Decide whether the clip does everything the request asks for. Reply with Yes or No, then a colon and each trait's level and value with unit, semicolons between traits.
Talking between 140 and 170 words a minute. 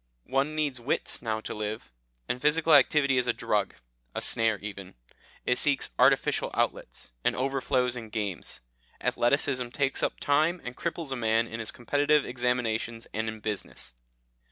Yes: average, 155 wpm